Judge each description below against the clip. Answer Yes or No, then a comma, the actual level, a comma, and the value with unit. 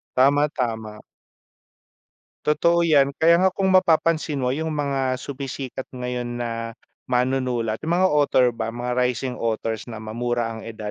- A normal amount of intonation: Yes, average, 4.0 semitones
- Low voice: Yes, low, 125 Hz